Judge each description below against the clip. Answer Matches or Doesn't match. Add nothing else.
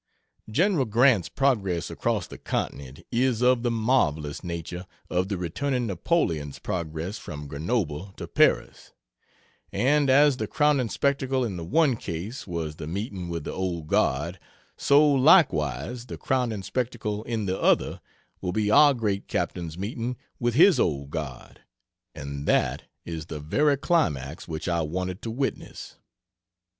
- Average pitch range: Doesn't match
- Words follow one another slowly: Doesn't match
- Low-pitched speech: Matches